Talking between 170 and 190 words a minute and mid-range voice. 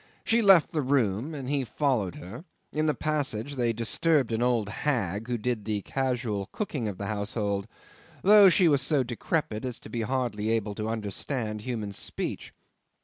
No: average, 175 wpm; low, 120 Hz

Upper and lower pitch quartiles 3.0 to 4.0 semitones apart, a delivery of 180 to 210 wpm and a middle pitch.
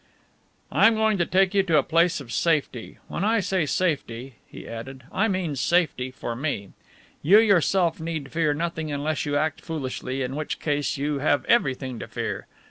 No: average, 4.8 semitones; average, 185 wpm; medium, 155 Hz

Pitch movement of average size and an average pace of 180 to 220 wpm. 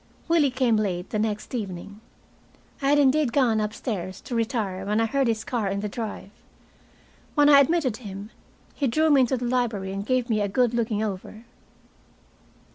Yes: average, 4.1 semitones; average, 185 wpm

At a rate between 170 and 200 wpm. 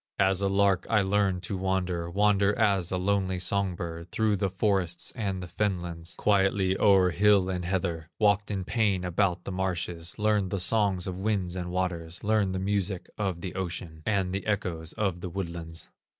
Yes: average, 180 wpm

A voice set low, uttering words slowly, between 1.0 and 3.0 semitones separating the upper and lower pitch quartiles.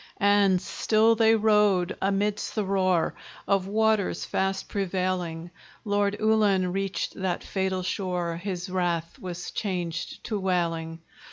No: high, 190 Hz; slow, 120 wpm; narrow, 2.4 semitones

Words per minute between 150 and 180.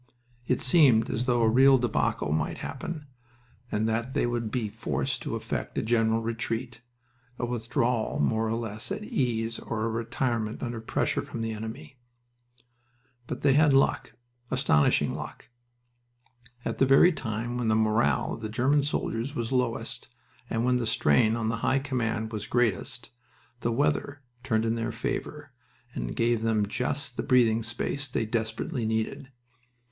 Yes: average, 160 wpm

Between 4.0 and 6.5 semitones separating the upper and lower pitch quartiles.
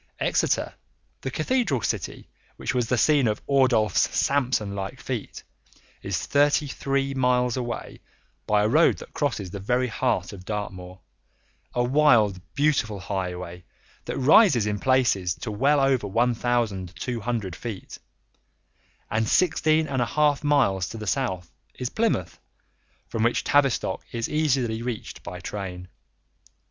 Yes: average, 5.1 semitones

